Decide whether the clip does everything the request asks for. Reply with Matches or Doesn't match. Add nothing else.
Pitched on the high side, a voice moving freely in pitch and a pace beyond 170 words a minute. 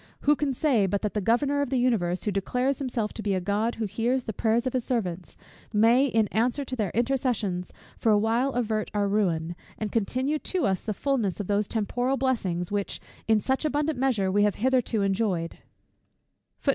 Doesn't match